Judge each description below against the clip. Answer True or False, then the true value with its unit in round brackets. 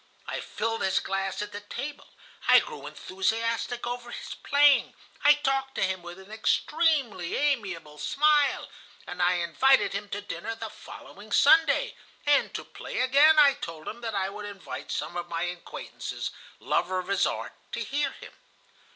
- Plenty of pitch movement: True (6.9 semitones)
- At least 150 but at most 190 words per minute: True (170 wpm)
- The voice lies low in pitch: False (220 Hz)